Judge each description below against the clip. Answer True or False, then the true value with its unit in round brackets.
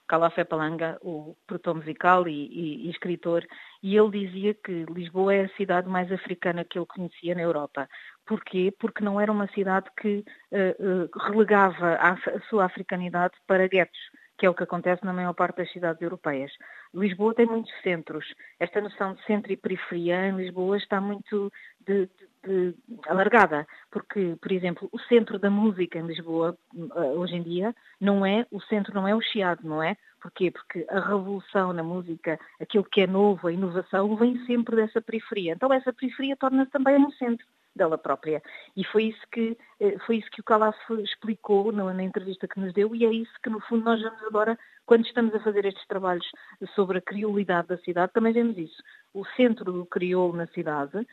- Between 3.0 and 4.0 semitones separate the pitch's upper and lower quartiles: True (3.5 semitones)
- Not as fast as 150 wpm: False (185 wpm)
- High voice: True (195 Hz)